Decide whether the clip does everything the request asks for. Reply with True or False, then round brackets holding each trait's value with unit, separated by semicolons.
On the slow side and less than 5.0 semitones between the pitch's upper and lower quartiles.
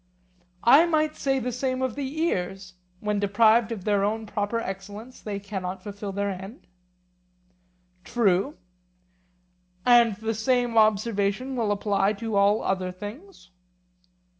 True (130 wpm; 3.4 semitones)